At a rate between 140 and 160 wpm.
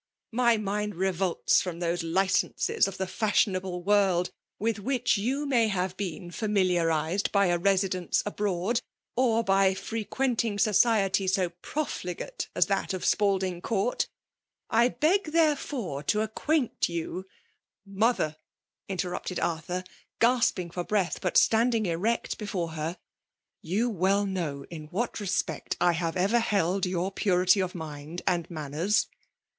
Yes: average, 150 wpm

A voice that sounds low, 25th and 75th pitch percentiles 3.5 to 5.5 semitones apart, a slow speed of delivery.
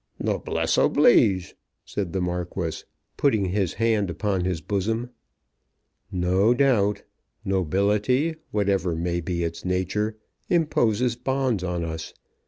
Yes: low, 100 Hz; average, 4.0 semitones; slow, 110 wpm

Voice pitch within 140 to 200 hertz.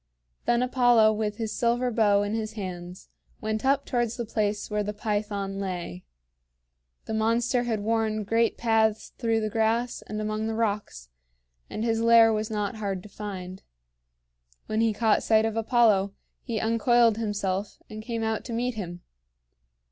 No: high, 220 Hz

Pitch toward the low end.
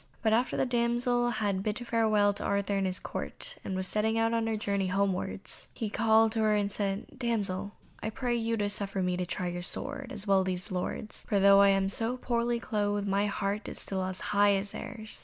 No: high, 205 Hz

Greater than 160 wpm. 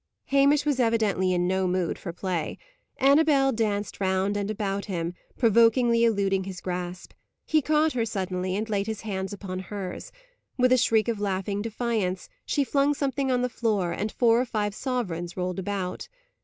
Yes: average, 170 wpm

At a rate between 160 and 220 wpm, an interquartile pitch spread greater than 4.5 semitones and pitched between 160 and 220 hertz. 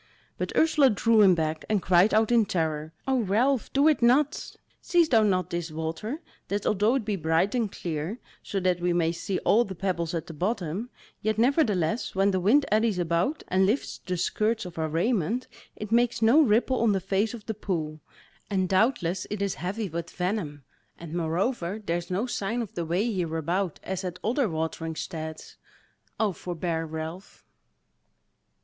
Yes: average, 180 wpm; average, 4.9 semitones; high, 190 Hz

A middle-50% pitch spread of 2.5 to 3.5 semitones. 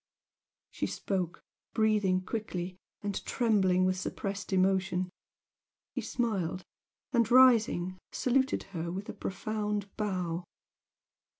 Yes: average, 2.8 semitones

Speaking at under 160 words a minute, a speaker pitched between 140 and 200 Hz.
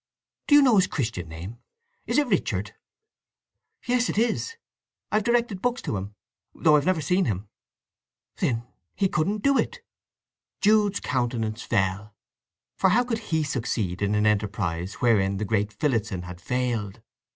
No: average, 145 wpm; low, 125 Hz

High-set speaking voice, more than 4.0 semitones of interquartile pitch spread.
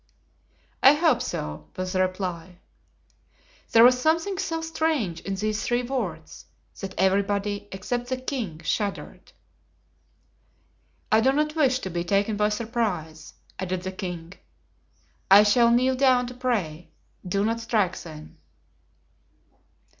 Yes: high, 210 Hz; average, 5.3 semitones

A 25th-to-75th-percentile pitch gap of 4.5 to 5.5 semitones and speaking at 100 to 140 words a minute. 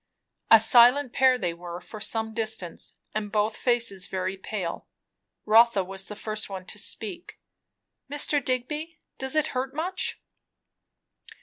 Yes: average, 5.1 semitones; slow, 135 wpm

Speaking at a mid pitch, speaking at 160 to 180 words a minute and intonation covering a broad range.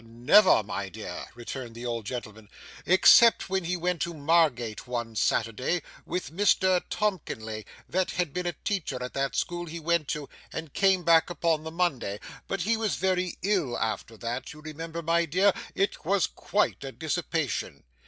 Yes: medium, 160 Hz; average, 170 wpm; wide, 6.7 semitones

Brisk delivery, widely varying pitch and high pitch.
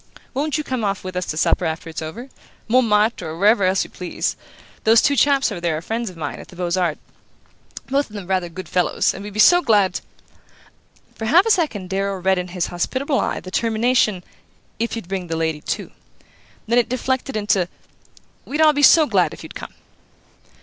Yes: fast, 210 wpm; wide, 5.8 semitones; high, 205 Hz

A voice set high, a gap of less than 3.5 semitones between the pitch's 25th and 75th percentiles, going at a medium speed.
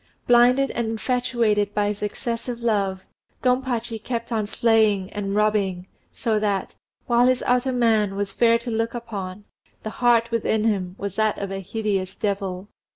Yes: high, 220 Hz; average, 2.9 semitones; average, 155 wpm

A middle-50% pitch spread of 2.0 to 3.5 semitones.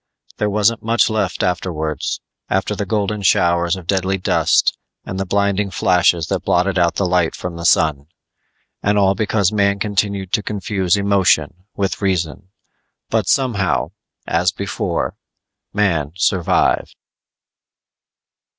Yes: narrow, 2.6 semitones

